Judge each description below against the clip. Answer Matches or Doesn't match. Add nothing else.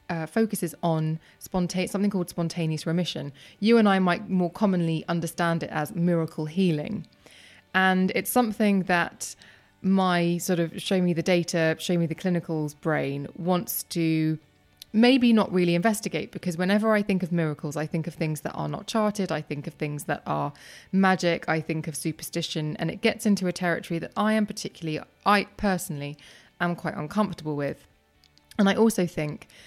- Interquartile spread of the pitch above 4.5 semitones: Doesn't match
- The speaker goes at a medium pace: Matches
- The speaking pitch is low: Doesn't match